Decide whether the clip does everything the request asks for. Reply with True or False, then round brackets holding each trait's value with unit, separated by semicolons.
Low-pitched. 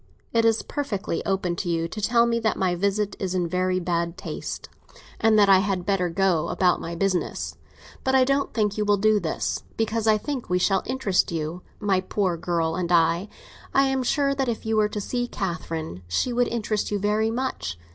False (200 Hz)